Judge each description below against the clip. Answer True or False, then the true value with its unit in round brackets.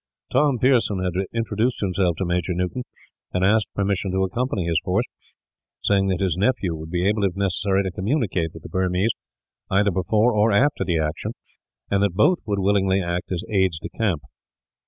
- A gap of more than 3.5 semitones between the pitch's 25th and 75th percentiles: False (2.9 semitones)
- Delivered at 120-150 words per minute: False (180 wpm)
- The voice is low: True (95 Hz)